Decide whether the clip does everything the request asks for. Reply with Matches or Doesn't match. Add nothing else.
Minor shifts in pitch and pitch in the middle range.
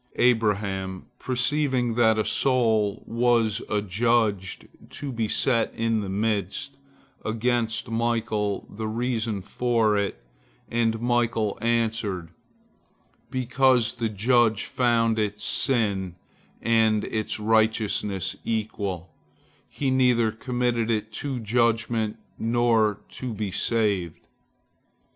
Doesn't match